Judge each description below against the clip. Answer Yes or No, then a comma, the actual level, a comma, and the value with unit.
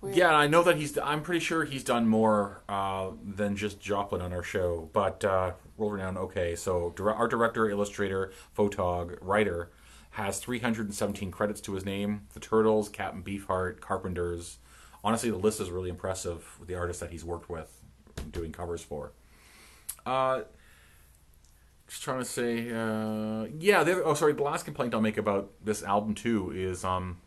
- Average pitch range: Yes, average, 3.9 semitones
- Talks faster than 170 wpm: No, average, 165 wpm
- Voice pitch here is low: Yes, low, 100 Hz